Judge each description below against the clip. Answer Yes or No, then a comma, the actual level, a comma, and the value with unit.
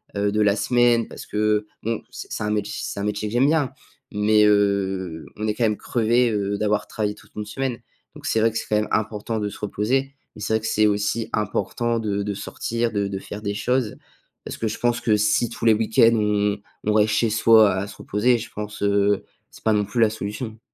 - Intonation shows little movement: Yes, narrow, 1.8 semitones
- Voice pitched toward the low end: Yes, low, 105 Hz